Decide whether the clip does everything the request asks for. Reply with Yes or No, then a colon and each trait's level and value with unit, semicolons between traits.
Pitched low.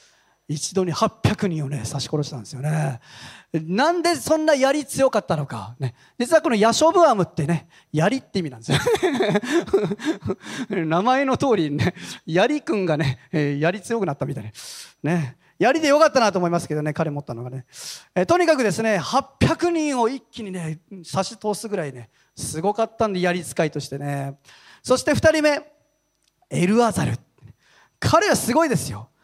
No: medium, 185 Hz